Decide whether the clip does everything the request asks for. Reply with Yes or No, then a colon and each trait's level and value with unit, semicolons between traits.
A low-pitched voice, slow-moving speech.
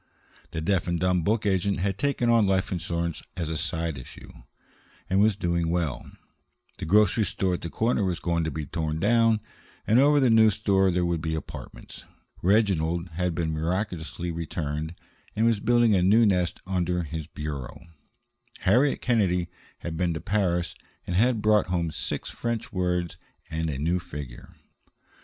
No: very low, 90 Hz; average, 170 wpm